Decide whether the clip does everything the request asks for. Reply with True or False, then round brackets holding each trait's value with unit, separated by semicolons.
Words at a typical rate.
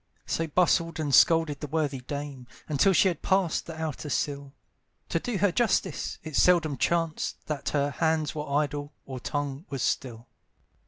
True (165 wpm)